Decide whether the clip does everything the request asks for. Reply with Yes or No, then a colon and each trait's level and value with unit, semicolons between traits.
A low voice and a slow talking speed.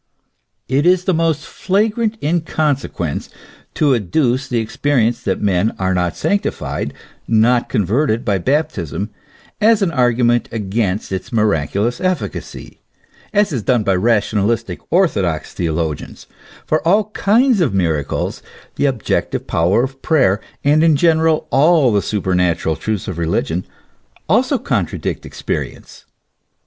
Yes: low, 120 Hz; slow, 130 wpm